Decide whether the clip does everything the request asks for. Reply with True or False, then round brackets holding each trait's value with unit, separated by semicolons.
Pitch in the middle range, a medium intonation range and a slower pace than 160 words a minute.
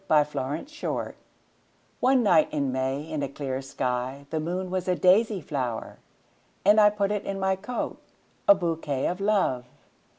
False (160 Hz; 6.1 semitones; 135 wpm)